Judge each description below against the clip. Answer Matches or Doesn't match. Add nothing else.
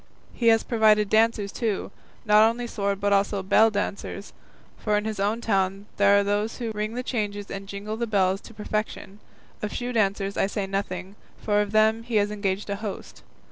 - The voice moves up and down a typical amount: Doesn't match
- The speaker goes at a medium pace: Matches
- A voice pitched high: Matches